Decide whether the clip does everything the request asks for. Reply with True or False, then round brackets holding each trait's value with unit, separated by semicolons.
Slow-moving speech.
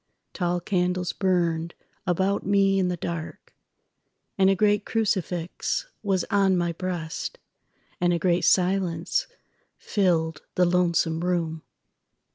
True (105 wpm)